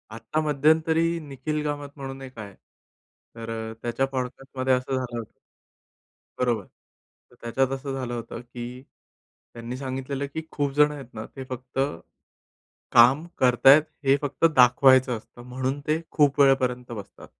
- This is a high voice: No, low, 130 Hz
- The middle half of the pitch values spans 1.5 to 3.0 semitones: Yes, narrow, 2.4 semitones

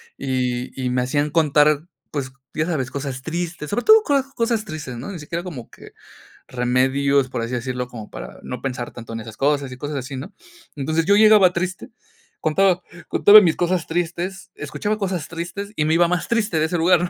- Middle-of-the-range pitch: Yes, medium, 155 Hz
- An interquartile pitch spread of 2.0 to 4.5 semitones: No, wide, 5.5 semitones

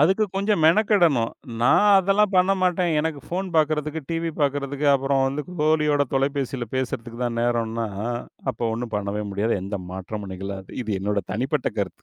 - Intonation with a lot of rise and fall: Yes, wide, 6.1 semitones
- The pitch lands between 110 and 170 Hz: Yes, medium, 140 Hz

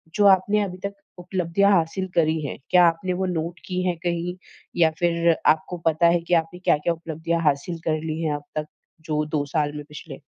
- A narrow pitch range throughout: Yes, narrow, 2.1 semitones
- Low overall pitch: No, medium, 170 Hz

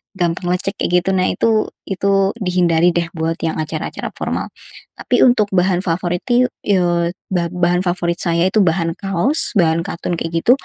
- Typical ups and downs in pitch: No, narrow, 2.3 semitones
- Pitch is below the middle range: No, medium, 180 Hz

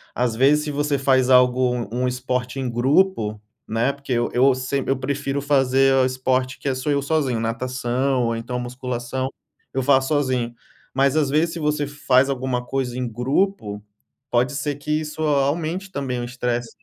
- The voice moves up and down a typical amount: No, narrow, 2.3 semitones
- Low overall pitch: Yes, low, 130 Hz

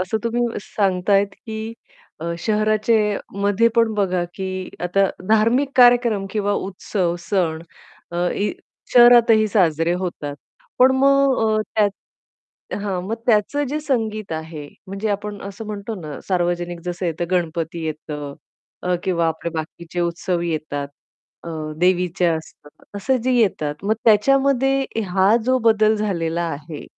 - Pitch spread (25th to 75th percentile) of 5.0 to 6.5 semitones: No, average, 4.3 semitones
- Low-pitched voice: No, high, 195 Hz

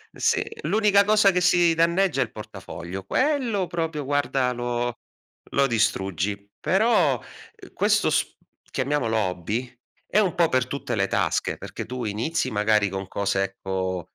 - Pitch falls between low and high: No, low, 125 Hz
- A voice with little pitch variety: No, wide, 8.9 semitones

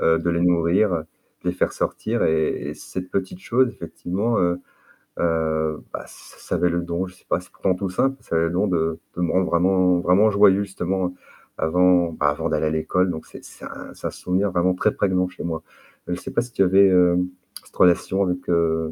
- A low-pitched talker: Yes, very low, 90 Hz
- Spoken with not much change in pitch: Yes, narrow, 2.1 semitones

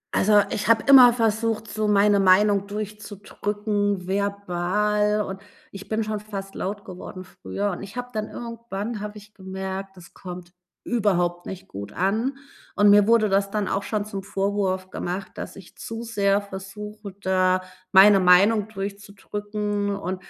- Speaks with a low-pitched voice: No, high, 205 Hz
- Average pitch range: No, narrow, 1.7 semitones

